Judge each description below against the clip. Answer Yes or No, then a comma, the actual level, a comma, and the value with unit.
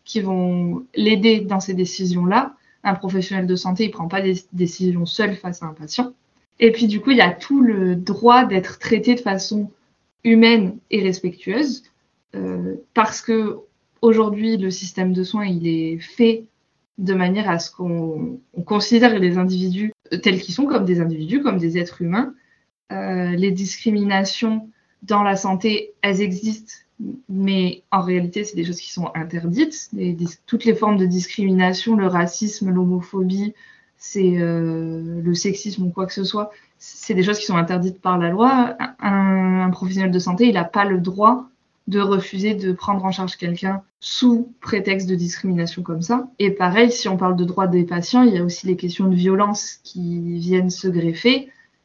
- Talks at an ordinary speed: Yes, average, 180 wpm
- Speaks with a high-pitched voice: Yes, high, 195 Hz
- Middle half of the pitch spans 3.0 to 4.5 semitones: Yes, average, 3.4 semitones